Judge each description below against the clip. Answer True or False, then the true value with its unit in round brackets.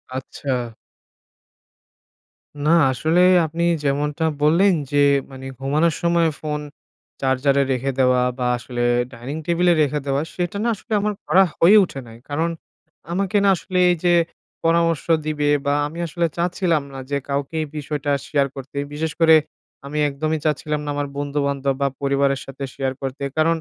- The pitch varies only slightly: False (3.2 semitones)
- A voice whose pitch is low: False (150 Hz)